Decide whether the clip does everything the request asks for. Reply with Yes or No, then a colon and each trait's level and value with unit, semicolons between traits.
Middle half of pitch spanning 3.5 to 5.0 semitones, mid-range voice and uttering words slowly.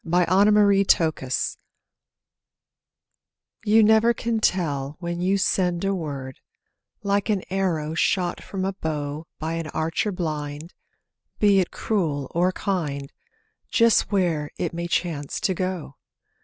Yes: average, 4.2 semitones; medium, 175 Hz; slow, 130 wpm